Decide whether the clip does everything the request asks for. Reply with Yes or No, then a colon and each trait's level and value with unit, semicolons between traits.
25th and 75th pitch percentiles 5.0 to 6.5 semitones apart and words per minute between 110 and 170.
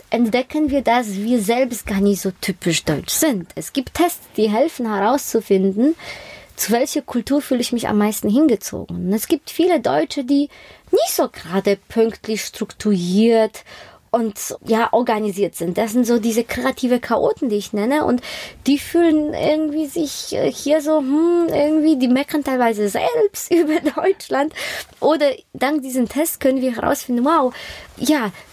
Yes: wide, 5.5 semitones; average, 155 wpm